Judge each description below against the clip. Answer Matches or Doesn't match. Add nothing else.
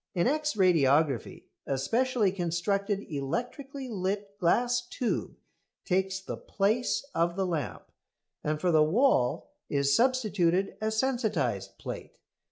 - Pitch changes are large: Matches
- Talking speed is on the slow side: Matches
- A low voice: Doesn't match